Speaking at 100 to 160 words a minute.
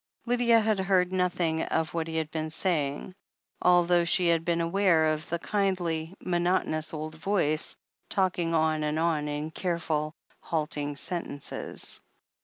Yes: average, 150 wpm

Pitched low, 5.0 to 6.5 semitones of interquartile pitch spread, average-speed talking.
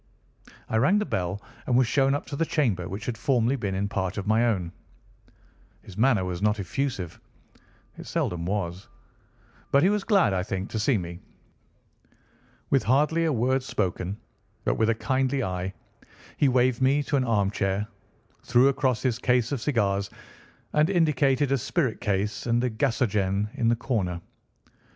Yes: low, 115 Hz; wide, 5.5 semitones; average, 165 wpm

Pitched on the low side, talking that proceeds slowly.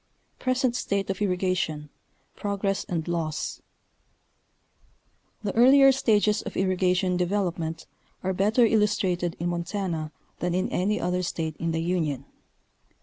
No: medium, 185 Hz; slow, 120 wpm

